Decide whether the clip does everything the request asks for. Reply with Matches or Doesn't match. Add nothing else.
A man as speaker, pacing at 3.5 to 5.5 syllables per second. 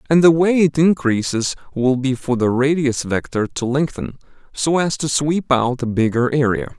Matches